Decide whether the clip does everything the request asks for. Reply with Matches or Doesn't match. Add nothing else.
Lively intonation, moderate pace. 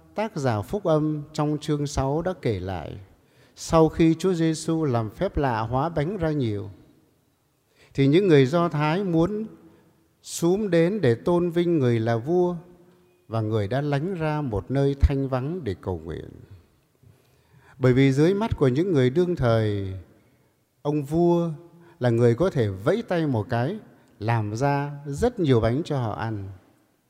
Matches